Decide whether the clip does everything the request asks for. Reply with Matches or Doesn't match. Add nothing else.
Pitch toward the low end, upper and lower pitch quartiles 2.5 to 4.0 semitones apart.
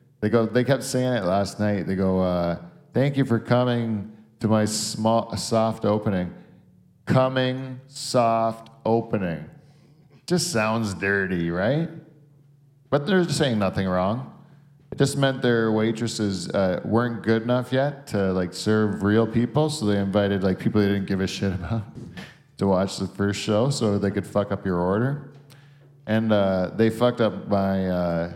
Doesn't match